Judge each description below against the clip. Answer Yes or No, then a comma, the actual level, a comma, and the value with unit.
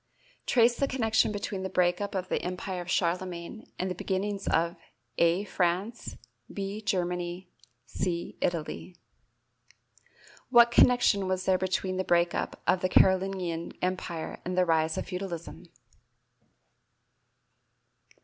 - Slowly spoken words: Yes, slow, 130 wpm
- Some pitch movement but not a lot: No, narrow, 2.2 semitones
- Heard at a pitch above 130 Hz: Yes, medium, 185 Hz